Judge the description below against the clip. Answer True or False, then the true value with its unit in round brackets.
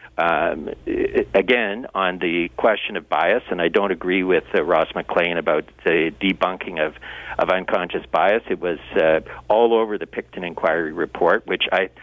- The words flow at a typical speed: True (170 wpm)